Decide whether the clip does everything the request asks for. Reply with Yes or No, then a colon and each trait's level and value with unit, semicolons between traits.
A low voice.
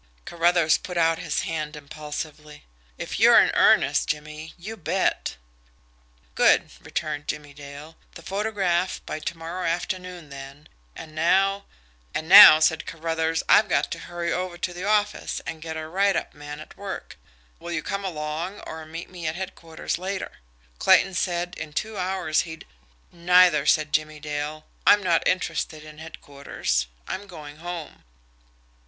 No: medium, 165 Hz